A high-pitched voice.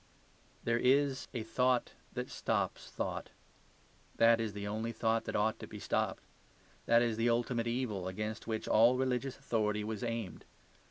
No: low, 115 Hz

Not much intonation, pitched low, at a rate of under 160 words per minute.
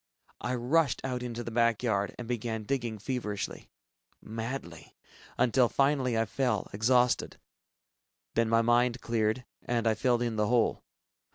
Yes: narrow, 2.0 semitones; low, 120 Hz; average, 145 wpm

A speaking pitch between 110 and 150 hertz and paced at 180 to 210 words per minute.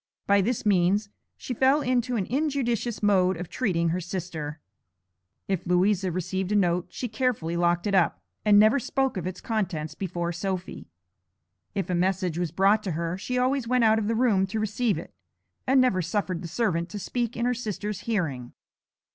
No: high, 195 Hz; average, 185 wpm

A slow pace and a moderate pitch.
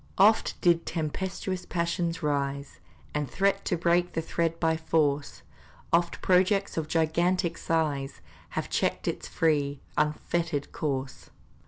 Yes: slow, 125 wpm; medium, 165 Hz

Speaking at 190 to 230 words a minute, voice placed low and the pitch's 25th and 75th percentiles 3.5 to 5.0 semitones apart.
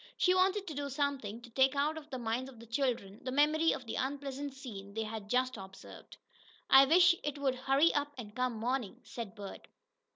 No: fast, 205 wpm; very high, 265 Hz; average, 4.0 semitones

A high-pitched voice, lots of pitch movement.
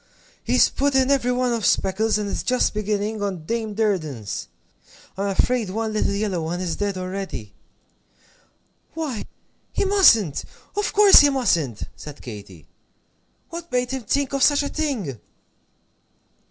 Yes: high, 215 Hz; wide, 6.0 semitones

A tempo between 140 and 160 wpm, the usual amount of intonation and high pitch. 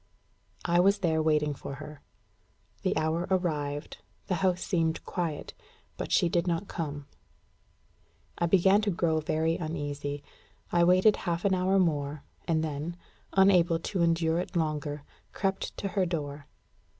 No: average, 145 wpm; average, 3.1 semitones; medium, 165 Hz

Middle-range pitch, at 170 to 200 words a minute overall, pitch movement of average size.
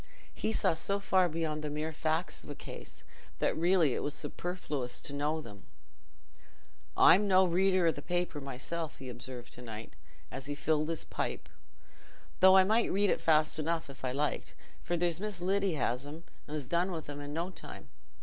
Yes: medium, 160 Hz; average, 195 wpm; average, 3.8 semitones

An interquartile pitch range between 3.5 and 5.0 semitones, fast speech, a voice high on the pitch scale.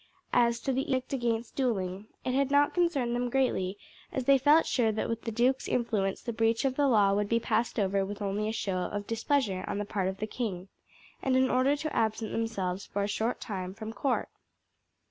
Yes: average, 4.3 semitones; fast, 215 wpm; high, 230 Hz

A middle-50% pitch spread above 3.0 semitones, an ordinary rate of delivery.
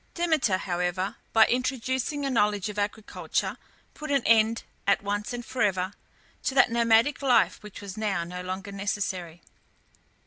Yes: average, 4.1 semitones; average, 150 wpm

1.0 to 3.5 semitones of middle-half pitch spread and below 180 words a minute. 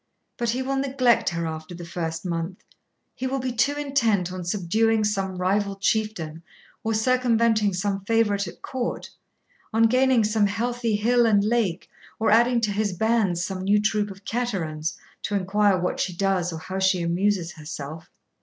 No: average, 4.1 semitones; average, 170 wpm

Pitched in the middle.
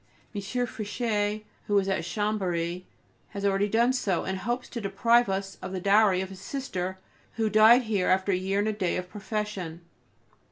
No: high, 200 Hz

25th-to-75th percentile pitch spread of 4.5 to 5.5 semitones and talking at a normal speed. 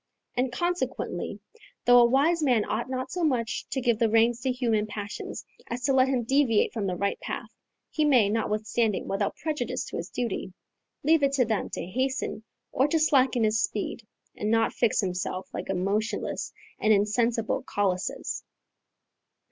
No: average, 3.8 semitones; average, 170 wpm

